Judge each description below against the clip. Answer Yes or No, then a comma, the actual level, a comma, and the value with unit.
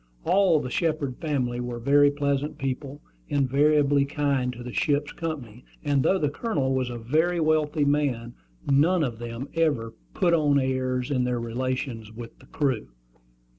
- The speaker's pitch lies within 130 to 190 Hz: Yes, medium, 140 Hz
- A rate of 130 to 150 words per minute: No, average, 160 wpm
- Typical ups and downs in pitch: Yes, average, 3.0 semitones